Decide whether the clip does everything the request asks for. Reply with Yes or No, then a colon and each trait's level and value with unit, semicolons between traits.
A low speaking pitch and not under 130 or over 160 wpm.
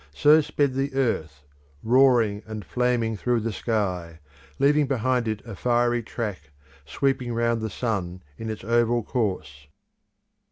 Yes: low, 115 Hz; slow, 135 wpm